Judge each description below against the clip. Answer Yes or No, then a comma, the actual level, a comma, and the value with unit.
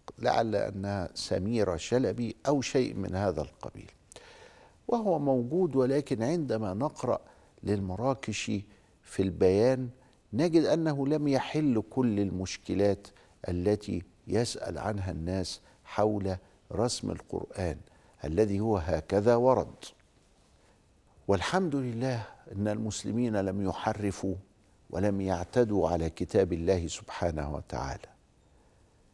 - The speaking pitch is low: Yes, low, 105 Hz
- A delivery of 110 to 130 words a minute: No, average, 95 wpm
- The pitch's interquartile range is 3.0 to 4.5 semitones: No, average, 5.3 semitones